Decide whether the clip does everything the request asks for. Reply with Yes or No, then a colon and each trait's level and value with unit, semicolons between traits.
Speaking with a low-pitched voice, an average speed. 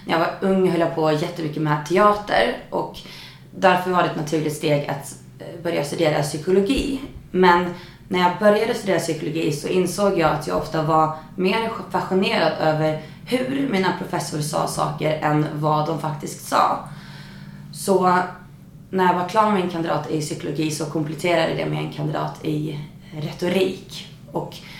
No: medium, 165 Hz; average, 160 wpm